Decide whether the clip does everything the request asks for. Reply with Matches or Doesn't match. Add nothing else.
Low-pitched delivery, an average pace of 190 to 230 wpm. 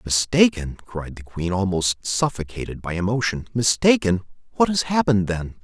Doesn't match